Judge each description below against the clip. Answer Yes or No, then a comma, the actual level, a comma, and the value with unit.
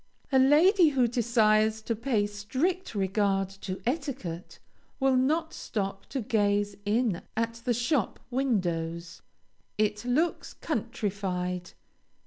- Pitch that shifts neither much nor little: Yes, average, 4.9 semitones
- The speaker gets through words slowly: Yes, slow, 115 wpm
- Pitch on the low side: No, high, 220 Hz